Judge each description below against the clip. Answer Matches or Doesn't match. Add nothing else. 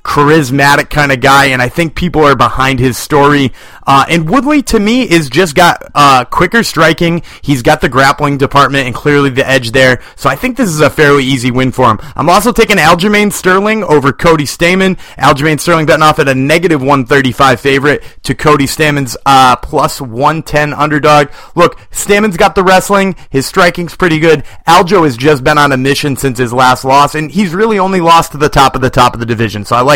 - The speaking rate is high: Matches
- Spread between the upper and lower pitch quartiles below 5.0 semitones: Matches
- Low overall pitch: Doesn't match